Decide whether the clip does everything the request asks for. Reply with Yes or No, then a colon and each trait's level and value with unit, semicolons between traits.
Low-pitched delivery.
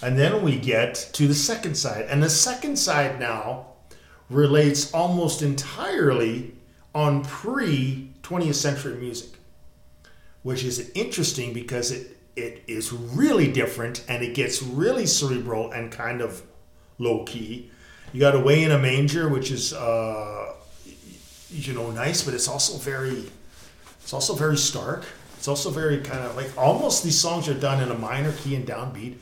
Yes: low, 130 Hz